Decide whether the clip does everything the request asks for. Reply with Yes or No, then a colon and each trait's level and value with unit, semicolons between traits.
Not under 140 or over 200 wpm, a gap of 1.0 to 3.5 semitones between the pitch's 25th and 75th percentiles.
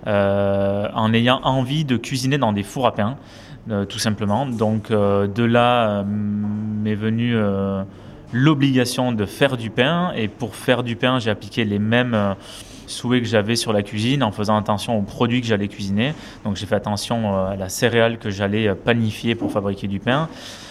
Yes: average, 190 wpm; average, 2.9 semitones